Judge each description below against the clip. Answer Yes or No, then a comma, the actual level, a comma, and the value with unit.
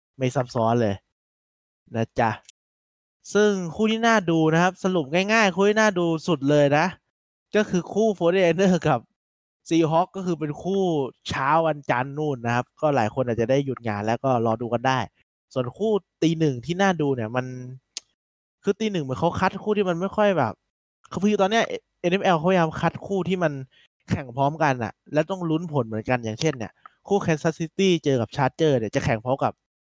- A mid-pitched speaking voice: Yes, medium, 155 Hz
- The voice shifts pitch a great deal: Yes, wide, 6.7 semitones